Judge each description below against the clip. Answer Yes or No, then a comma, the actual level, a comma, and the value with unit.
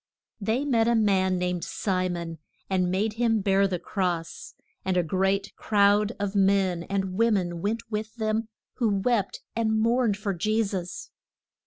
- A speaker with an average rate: Yes, average, 165 wpm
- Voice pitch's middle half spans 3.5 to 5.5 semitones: No, average, 2.9 semitones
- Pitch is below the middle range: No, high, 200 Hz